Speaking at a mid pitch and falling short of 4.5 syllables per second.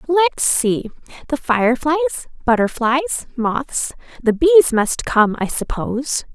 No: very high, 265 Hz; 4.0 syllables/s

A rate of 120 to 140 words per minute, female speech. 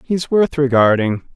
No: slow, 135 wpm; male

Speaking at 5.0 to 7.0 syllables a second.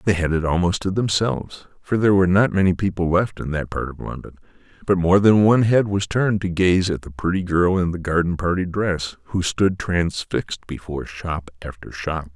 Yes: 5.4 syllables/s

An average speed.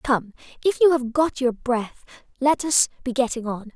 Yes: average, 190 wpm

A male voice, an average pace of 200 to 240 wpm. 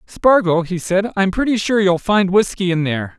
Yes: male; fast, 205 wpm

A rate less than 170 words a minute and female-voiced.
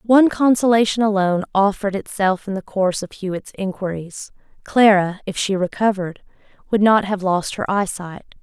Yes: average, 150 wpm; female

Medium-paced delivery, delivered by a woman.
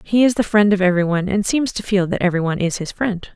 No: fast, 270 wpm; female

